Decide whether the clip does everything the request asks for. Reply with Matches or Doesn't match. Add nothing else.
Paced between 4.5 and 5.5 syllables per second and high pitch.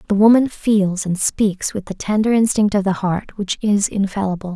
Matches